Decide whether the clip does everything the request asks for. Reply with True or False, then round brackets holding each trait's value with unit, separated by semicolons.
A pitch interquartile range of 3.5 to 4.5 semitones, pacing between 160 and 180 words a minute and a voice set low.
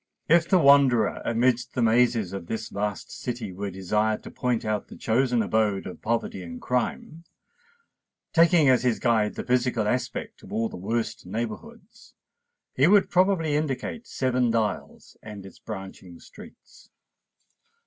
False (4.0 semitones; 150 wpm; 115 Hz)